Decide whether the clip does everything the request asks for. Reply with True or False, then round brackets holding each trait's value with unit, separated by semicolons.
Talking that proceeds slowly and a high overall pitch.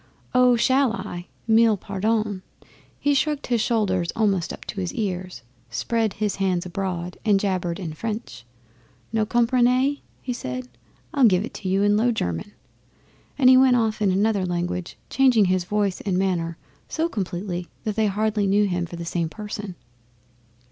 False (160 wpm; 205 Hz)